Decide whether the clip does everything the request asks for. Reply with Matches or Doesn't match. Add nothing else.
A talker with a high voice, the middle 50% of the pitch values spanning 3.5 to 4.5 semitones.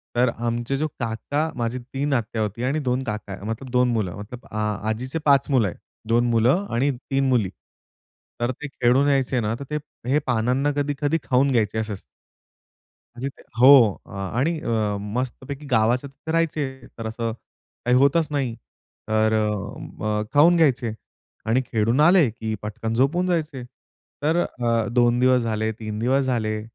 Doesn't match